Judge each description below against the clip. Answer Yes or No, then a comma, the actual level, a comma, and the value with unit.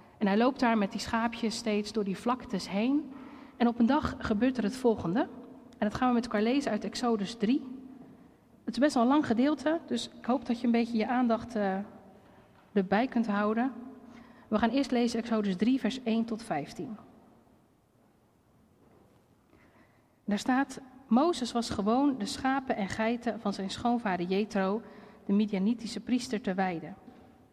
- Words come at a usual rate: Yes, average, 170 wpm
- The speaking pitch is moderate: No, high, 235 Hz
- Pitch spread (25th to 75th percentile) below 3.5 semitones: Yes, average, 3.0 semitones